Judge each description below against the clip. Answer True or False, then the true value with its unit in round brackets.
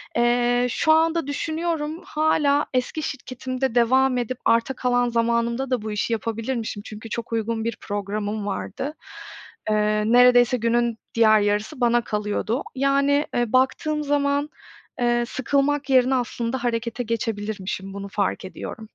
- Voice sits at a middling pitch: False (240 Hz)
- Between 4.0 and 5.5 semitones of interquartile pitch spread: False (3.2 semitones)